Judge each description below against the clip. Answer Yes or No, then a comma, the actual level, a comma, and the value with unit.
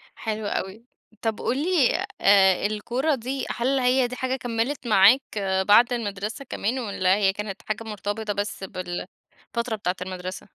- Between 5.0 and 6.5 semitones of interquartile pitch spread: No, average, 3.9 semitones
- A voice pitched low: No, high, 220 Hz